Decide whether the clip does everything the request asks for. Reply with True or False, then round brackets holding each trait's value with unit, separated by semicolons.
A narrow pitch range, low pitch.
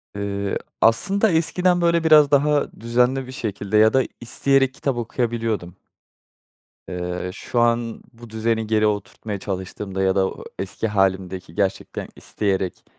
False (5.2 semitones; 110 Hz)